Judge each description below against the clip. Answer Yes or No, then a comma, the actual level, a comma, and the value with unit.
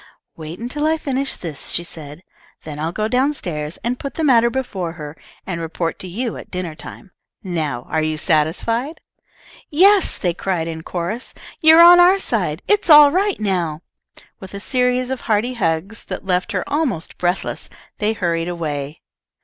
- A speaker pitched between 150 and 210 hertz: Yes, high, 190 Hz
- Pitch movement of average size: No, wide, 7.7 semitones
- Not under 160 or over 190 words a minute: Yes, average, 175 wpm